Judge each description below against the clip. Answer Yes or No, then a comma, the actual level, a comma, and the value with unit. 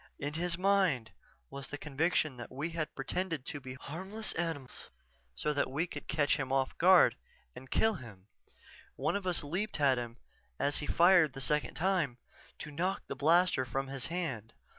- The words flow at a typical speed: Yes, average, 180 wpm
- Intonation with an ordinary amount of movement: Yes, average, 4.6 semitones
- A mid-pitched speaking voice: Yes, medium, 150 Hz